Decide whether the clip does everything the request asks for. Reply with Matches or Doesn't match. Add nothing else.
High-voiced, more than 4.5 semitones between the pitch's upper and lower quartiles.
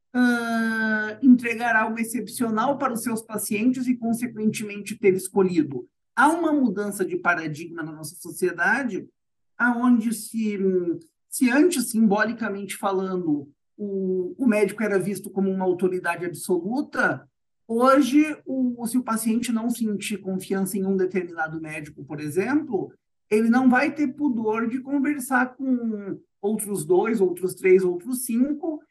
Matches